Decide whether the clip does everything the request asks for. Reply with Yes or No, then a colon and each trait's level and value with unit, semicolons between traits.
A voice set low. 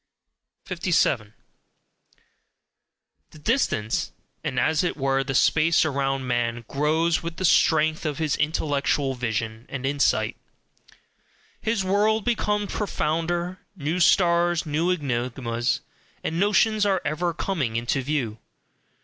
No: medium, 155 Hz